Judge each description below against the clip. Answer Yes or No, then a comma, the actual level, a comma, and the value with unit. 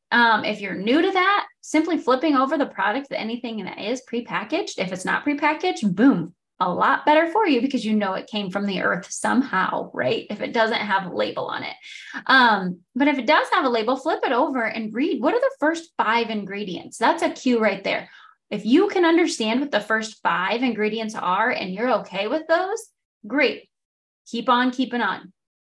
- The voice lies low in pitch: No, very high, 250 Hz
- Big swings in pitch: Yes, wide, 6.4 semitones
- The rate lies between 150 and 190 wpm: No, fast, 205 wpm